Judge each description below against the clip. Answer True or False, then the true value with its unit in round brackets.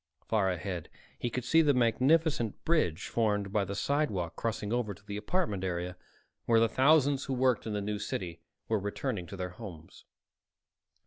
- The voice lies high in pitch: False (105 Hz)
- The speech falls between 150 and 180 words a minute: True (175 wpm)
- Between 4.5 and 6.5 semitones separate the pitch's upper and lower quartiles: True (4.8 semitones)